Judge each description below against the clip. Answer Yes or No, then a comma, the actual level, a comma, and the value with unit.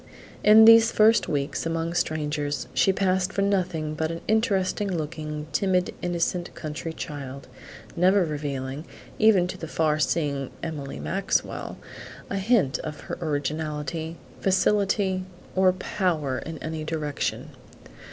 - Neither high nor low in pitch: Yes, medium, 165 Hz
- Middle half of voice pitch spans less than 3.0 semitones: No, average, 3.8 semitones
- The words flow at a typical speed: No, slow, 125 wpm